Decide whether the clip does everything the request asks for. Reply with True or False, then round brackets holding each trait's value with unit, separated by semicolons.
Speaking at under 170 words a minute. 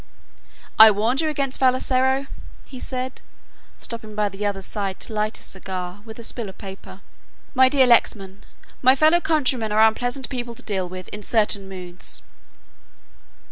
True (160 wpm)